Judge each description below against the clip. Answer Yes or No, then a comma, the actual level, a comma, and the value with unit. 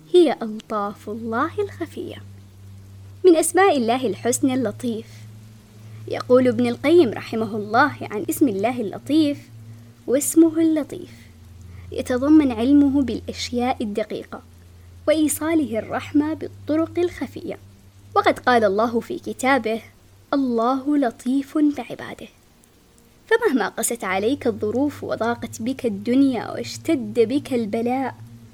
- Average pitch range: No, wide, 8.1 semitones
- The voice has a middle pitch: No, high, 240 Hz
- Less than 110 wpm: Yes, average, 95 wpm